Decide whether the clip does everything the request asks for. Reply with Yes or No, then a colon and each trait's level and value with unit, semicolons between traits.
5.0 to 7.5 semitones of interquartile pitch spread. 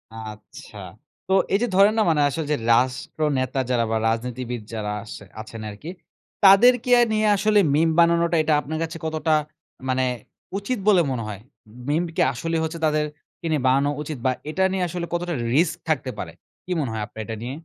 Yes: wide, 5.4 semitones